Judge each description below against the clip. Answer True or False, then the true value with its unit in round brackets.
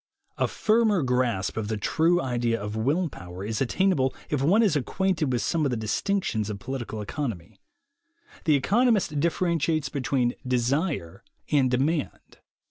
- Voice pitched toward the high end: False (135 Hz)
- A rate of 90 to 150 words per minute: True (145 wpm)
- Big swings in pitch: True (6.5 semitones)